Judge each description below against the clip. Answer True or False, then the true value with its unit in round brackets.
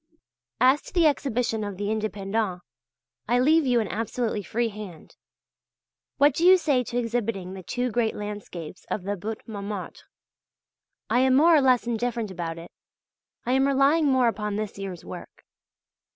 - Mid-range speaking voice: False (225 Hz)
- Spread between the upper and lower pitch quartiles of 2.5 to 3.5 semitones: False (4.0 semitones)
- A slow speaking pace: False (165 wpm)